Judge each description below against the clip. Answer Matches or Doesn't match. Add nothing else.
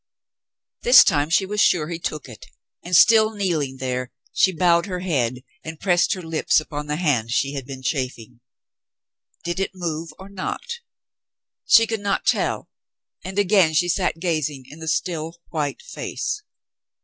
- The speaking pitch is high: Doesn't match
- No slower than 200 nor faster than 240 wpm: Doesn't match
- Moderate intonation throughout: Matches